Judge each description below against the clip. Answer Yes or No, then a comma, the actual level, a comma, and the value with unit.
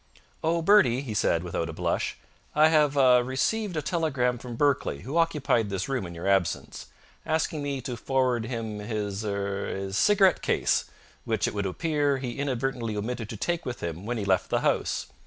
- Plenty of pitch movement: Yes, wide, 6.0 semitones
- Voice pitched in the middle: No, low, 125 Hz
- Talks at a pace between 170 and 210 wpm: Yes, average, 190 wpm